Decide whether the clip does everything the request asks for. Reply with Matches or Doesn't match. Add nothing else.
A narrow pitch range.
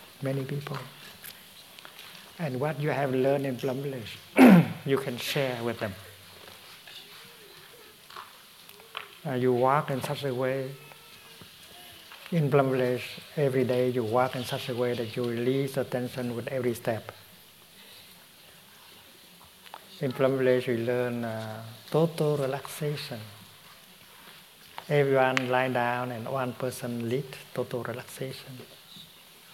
Matches